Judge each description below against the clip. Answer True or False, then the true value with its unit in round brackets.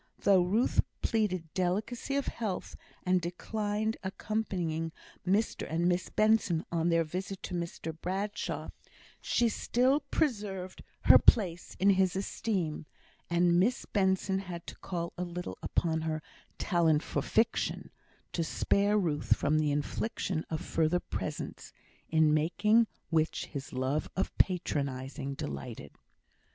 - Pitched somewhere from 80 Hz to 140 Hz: False (180 Hz)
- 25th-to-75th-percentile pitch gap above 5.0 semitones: False (4.2 semitones)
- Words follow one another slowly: True (130 wpm)